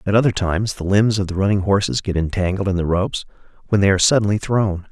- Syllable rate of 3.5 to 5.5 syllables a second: No, 6.7 syllables/s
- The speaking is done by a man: Yes, male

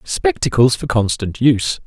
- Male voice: Yes, male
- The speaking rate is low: Yes, slow, 130 wpm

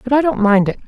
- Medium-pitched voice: No, high, 240 Hz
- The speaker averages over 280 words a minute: Yes, fast, 340 wpm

